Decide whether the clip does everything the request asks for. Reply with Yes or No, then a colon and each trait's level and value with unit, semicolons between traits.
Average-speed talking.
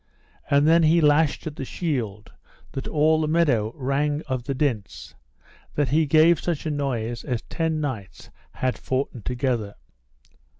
Yes: average, 155 wpm